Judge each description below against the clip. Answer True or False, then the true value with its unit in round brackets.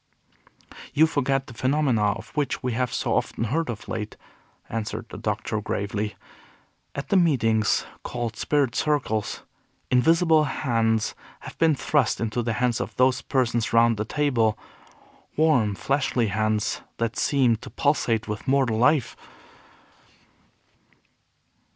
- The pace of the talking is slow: True (130 wpm)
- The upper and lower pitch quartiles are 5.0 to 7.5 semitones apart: False (4.2 semitones)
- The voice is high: False (120 Hz)